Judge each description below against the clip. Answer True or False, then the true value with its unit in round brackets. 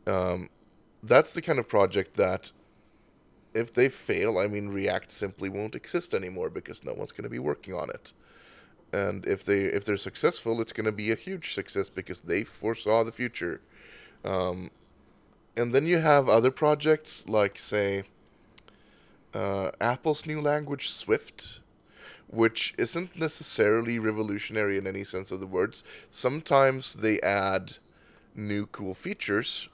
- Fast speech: False (145 wpm)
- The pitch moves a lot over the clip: True (6.2 semitones)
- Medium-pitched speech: False (110 Hz)